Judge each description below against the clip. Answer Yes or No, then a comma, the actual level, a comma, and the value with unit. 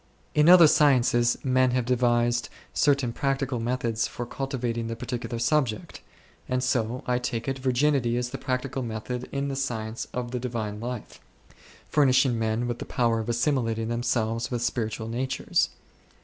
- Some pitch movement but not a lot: No, narrow, 2.1 semitones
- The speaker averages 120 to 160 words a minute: Yes, average, 155 wpm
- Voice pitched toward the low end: Yes, low, 120 Hz